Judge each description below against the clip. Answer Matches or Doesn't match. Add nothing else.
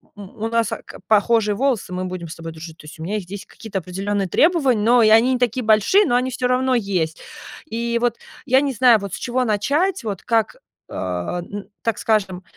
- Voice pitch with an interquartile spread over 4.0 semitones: Matches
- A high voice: Matches